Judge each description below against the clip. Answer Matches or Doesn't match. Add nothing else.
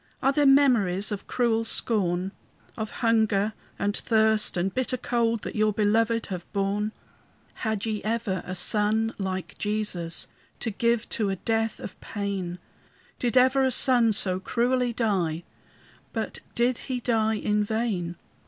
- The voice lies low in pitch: Doesn't match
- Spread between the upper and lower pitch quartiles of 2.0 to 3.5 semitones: Matches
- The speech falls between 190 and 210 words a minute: Doesn't match